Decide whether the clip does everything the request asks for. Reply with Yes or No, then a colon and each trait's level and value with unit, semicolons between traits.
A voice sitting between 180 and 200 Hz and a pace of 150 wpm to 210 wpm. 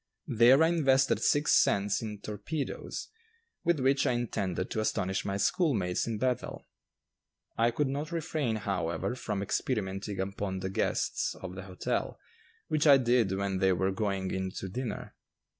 No: low, 110 Hz; average, 155 wpm